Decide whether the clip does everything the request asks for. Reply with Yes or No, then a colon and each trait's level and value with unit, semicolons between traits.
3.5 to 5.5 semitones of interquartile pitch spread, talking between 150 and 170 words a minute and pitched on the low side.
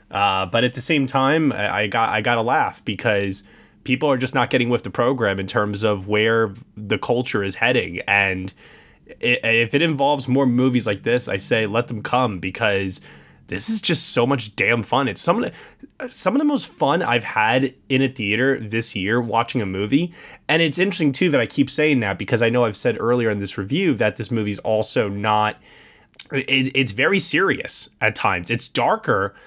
No: average, 4.3 semitones; fast, 205 wpm; low, 120 Hz